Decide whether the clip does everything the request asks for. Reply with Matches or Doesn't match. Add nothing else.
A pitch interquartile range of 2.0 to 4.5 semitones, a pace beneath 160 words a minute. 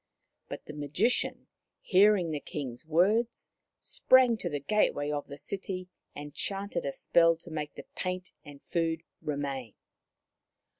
Doesn't match